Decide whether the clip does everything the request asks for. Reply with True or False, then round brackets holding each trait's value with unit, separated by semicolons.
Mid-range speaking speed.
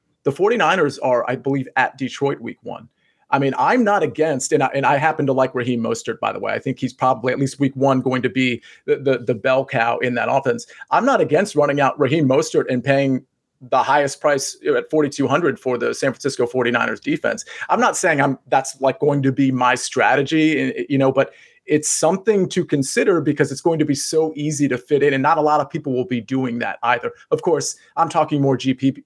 False (225 wpm)